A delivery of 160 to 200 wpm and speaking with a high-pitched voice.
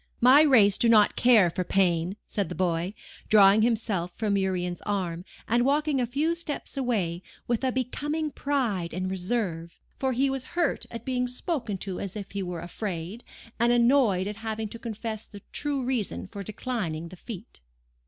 Yes: average, 175 wpm; high, 215 Hz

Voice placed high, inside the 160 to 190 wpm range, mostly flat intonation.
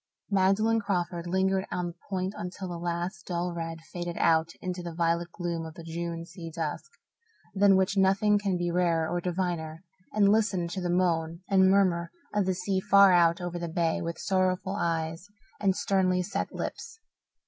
No: medium, 180 Hz; average, 180 wpm; narrow, 2.1 semitones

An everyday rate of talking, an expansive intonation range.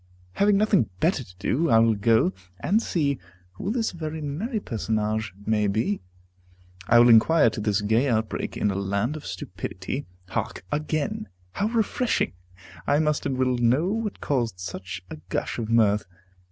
Yes: average, 165 wpm; wide, 6.9 semitones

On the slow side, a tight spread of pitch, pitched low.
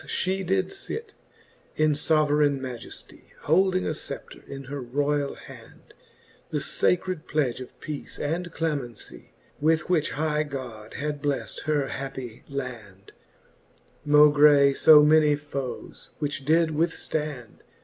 No: slow, 125 wpm; narrow, 2.3 semitones; medium, 150 Hz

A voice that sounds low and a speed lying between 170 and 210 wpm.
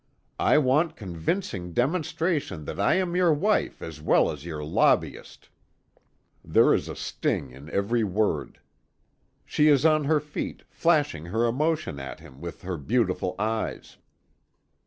No: low, 115 Hz; average, 140 wpm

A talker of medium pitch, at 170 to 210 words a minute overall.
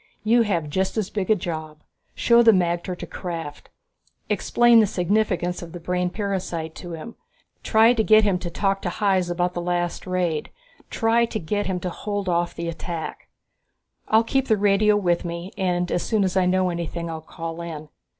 Yes: medium, 180 Hz; average, 190 wpm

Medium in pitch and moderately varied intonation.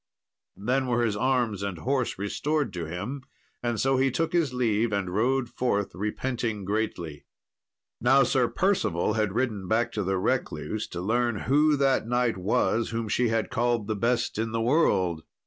No: low, 115 Hz; average, 3.9 semitones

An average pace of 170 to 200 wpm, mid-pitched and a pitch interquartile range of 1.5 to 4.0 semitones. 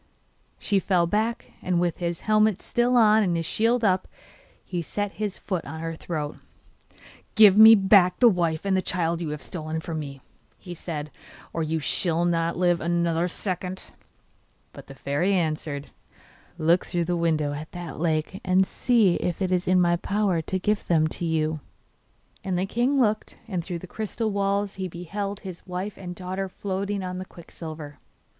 Yes: average, 180 wpm; medium, 180 Hz; average, 3.2 semitones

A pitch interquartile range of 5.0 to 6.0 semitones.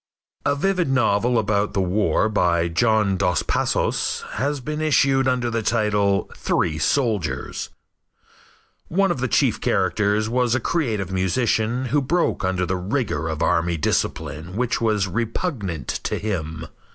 Yes: wide, 5.6 semitones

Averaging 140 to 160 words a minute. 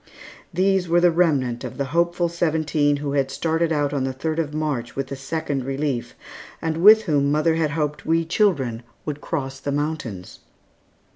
No: average, 175 wpm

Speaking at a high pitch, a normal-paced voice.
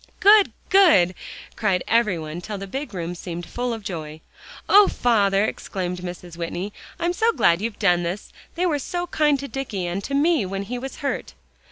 Yes: high, 205 Hz; average, 190 wpm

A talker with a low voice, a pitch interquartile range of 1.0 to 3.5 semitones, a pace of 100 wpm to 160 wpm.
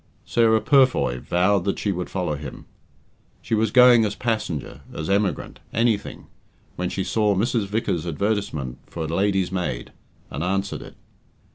No: low, 100 Hz; average, 4.2 semitones; average, 150 wpm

